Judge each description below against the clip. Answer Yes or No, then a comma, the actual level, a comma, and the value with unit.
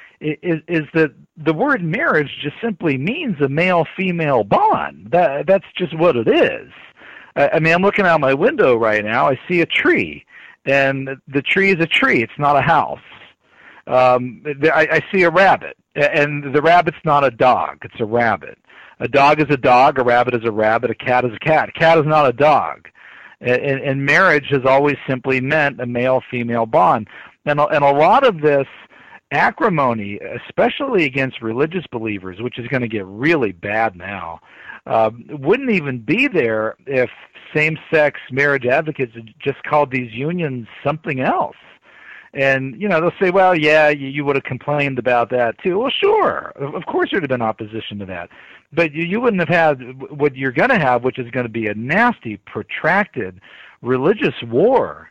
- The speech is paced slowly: No, average, 185 wpm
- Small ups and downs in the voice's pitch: No, average, 4.5 semitones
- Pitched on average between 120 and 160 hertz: Yes, medium, 140 Hz